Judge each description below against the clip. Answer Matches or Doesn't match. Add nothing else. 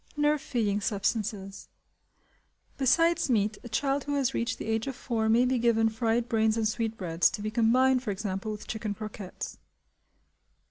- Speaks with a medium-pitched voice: Doesn't match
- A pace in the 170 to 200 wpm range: Doesn't match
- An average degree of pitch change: Matches